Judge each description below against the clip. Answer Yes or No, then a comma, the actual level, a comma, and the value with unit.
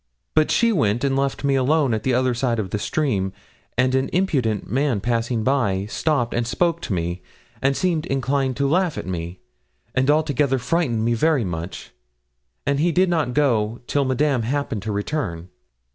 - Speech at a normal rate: Yes, average, 180 wpm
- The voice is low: Yes, low, 130 Hz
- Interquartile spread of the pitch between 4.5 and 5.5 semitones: Yes, average, 4.9 semitones